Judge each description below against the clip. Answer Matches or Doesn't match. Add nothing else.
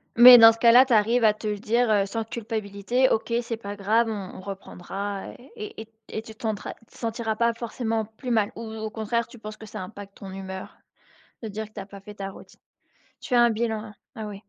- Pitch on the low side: Doesn't match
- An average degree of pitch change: Doesn't match